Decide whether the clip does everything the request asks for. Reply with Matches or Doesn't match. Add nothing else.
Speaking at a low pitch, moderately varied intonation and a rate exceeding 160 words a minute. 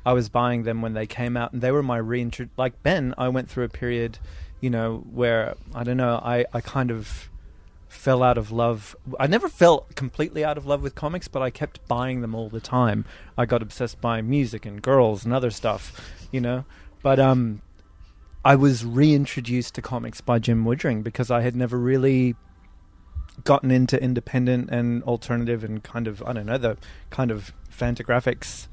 Doesn't match